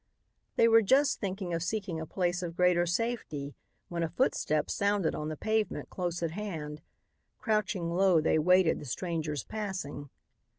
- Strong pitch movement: No, average, 4.1 semitones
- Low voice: No, medium, 175 Hz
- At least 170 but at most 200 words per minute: No, average, 160 wpm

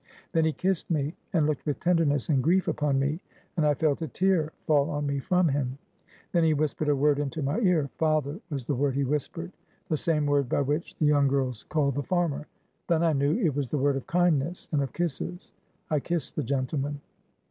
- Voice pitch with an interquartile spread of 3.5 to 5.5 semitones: No, average, 2.7 semitones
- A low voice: No, medium, 150 Hz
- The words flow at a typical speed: No, fast, 215 wpm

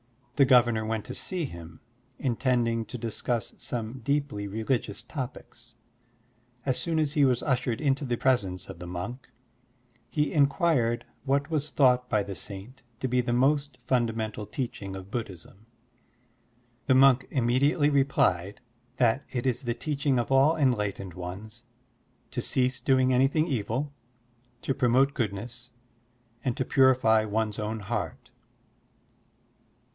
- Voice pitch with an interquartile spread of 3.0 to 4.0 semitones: Yes, average, 3.7 semitones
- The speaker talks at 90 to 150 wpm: Yes, slow, 135 wpm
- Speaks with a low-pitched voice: Yes, low, 125 Hz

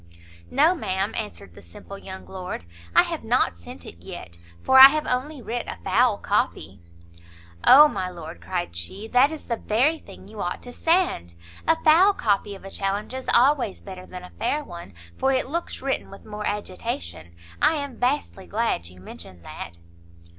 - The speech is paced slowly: No, average, 185 wpm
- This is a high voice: Yes, high, 210 Hz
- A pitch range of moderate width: No, wide, 7.5 semitones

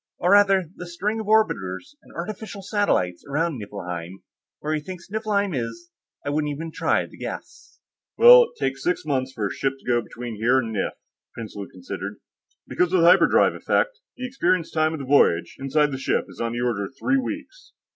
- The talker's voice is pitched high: No, medium, 155 Hz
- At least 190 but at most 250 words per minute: Yes, average, 195 wpm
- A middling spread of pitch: No, wide, 9.0 semitones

